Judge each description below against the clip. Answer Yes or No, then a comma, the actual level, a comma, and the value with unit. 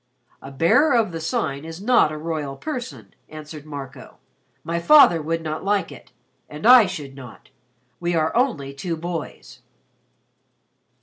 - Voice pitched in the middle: Yes, medium, 160 Hz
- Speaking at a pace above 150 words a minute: No, average, 145 wpm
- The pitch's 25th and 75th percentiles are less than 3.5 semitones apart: No, average, 3.9 semitones